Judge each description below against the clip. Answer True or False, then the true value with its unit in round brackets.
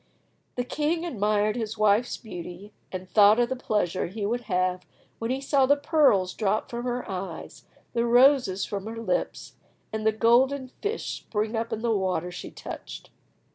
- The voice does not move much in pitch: False (4.0 semitones)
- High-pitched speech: True (220 Hz)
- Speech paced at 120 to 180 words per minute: True (175 wpm)